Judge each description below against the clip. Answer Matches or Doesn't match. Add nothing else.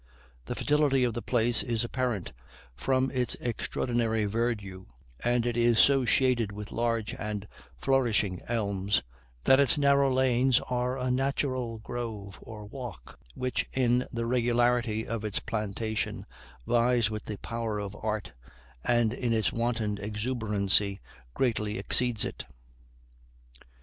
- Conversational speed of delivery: Doesn't match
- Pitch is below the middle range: Matches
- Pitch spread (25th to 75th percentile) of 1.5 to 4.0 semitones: Matches